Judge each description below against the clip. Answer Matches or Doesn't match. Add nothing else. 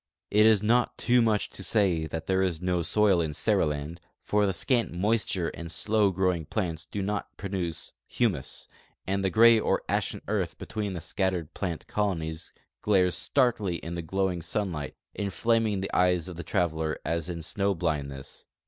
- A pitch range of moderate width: Matches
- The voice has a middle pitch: Doesn't match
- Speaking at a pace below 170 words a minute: Doesn't match